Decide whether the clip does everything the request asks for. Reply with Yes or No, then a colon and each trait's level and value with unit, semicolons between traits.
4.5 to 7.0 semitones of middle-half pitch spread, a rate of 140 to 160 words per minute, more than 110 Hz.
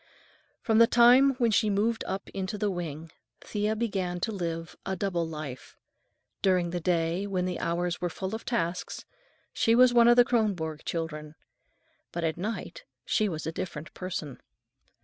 No: average, 4.8 semitones; average, 170 wpm; medium, 185 Hz